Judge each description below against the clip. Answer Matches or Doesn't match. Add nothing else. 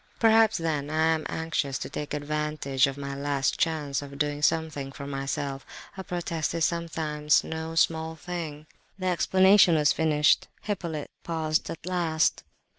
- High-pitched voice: Doesn't match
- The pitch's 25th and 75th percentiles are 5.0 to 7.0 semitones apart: Doesn't match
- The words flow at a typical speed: Matches